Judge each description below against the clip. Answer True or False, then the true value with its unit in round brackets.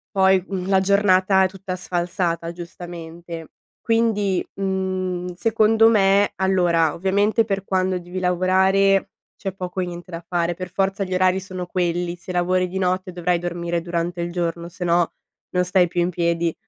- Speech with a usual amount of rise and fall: False (1.7 semitones)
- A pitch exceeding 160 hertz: True (185 Hz)